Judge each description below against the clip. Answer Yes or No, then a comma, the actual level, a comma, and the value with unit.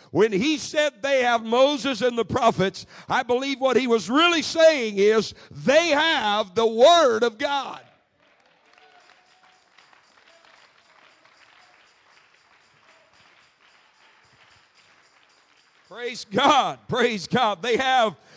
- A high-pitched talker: Yes, high, 245 Hz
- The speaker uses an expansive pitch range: No, average, 4.1 semitones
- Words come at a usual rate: No, slow, 95 wpm